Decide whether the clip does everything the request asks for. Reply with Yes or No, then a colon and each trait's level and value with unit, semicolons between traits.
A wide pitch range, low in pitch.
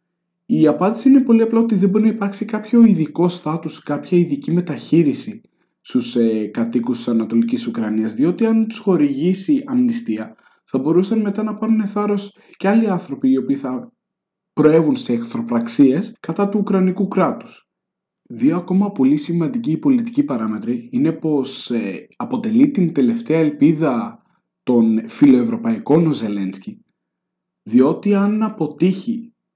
No: wide, 7.3 semitones; medium, 185 Hz